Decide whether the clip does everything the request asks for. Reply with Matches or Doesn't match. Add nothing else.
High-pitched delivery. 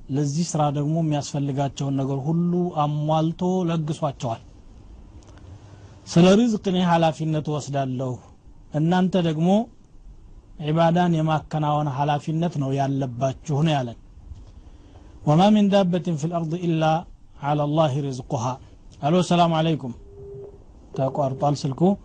Doesn't match